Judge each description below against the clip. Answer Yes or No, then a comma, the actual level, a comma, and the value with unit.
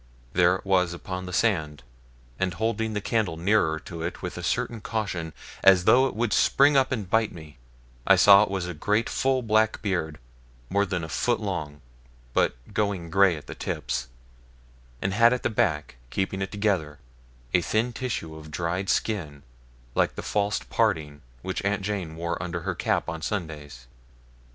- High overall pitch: No, very low, 95 Hz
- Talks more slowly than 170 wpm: No, average, 180 wpm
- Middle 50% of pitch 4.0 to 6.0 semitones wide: Yes, average, 4.6 semitones